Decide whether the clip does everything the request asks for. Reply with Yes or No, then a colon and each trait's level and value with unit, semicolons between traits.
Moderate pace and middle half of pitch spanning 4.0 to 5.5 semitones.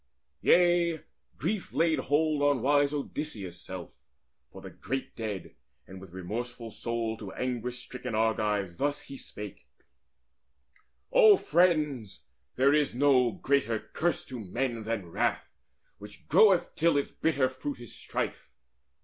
No: slow, 130 wpm; average, 5.2 semitones